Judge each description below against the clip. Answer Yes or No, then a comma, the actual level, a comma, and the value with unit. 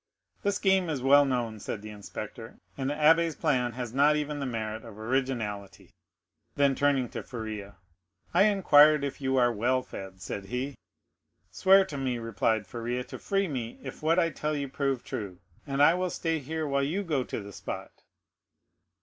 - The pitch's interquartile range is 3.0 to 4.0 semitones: No, average, 4.8 semitones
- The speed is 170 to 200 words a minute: Yes, average, 185 wpm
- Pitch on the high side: No, low, 135 Hz